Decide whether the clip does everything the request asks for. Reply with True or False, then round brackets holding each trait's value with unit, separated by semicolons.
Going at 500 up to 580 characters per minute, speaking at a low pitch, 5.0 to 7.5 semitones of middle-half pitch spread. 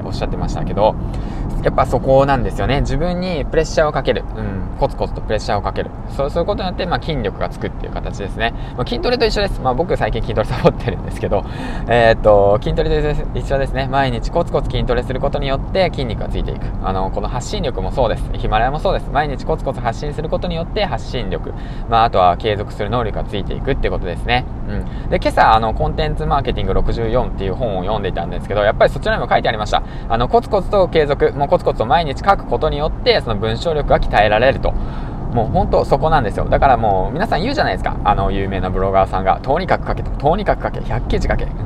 True (515 characters per minute; 125 Hz; 5.7 semitones)